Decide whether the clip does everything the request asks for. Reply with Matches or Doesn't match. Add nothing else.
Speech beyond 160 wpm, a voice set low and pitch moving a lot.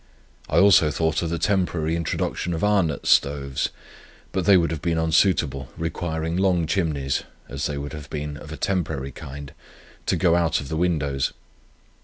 Doesn't match